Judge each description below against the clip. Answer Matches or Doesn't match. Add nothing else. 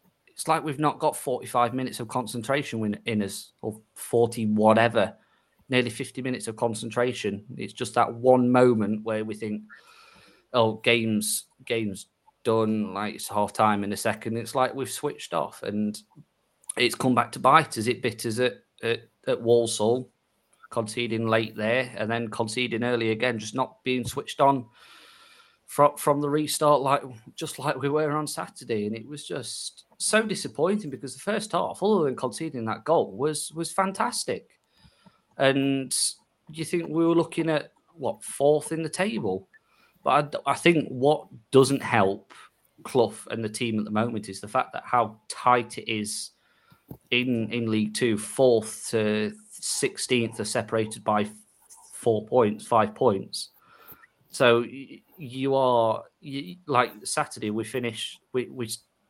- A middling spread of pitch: Matches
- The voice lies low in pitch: Matches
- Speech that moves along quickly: Doesn't match